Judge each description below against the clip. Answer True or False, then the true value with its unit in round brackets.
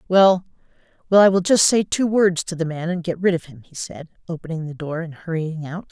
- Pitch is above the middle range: False (170 Hz)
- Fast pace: True (245 wpm)